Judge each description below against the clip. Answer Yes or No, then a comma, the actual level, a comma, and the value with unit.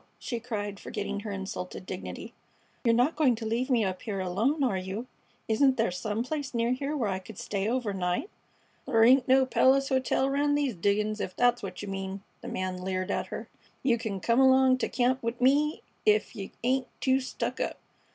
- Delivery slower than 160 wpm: No, average, 200 wpm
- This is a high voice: Yes, high, 230 Hz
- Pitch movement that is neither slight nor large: Yes, average, 4.7 semitones